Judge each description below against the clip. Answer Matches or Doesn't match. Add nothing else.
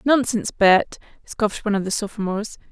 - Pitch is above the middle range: Matches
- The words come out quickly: Doesn't match